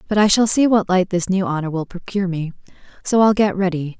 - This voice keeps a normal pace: No, fast, 225 wpm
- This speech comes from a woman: Yes, female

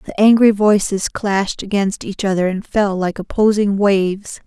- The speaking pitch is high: Yes, high, 200 Hz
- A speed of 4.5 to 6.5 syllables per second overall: Yes, 4.7 syllables/s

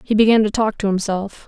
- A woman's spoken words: Yes, female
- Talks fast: Yes, fast, 245 wpm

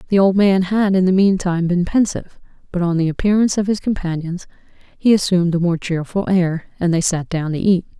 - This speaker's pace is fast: Yes, fast, 210 wpm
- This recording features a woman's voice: Yes, female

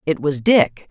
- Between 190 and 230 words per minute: Yes, average, 200 wpm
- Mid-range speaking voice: Yes, medium, 160 Hz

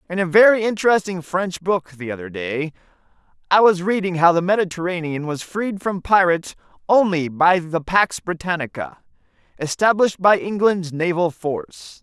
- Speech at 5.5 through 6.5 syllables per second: No, 5.0 syllables/s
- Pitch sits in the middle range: Yes, medium, 175 Hz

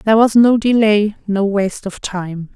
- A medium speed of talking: Yes, average, 190 wpm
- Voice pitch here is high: Yes, high, 205 Hz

